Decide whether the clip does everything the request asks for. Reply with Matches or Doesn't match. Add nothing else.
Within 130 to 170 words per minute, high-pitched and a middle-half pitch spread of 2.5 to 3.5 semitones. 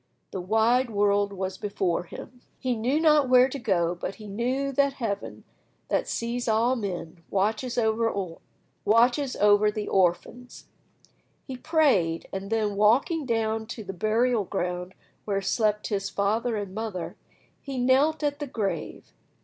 Doesn't match